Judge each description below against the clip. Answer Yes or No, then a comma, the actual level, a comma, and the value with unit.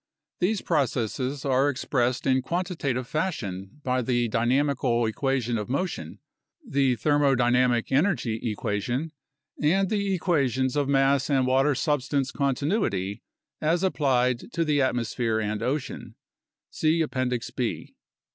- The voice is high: No, low, 130 Hz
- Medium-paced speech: No, slow, 120 wpm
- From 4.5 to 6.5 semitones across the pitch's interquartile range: No, average, 3.5 semitones